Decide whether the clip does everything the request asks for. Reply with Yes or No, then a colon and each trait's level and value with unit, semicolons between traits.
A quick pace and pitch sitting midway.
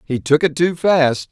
Yes: fast, 230 wpm; medium, 155 Hz